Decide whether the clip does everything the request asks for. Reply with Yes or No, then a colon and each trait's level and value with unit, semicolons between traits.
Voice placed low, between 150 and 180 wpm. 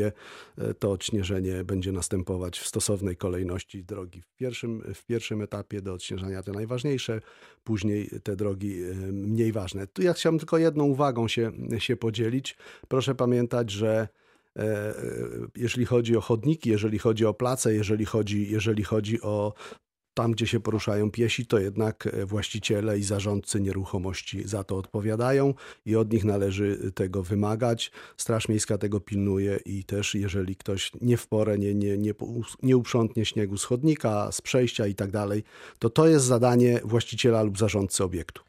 Yes: low, 110 Hz; average, 155 wpm